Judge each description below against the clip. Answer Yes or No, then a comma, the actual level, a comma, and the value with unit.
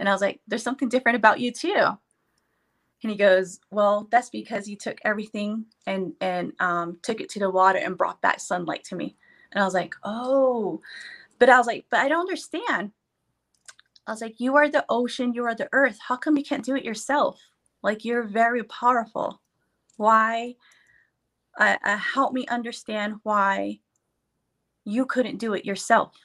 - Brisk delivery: No, average, 180 wpm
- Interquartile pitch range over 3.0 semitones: Yes, average, 3.5 semitones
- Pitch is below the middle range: No, high, 230 Hz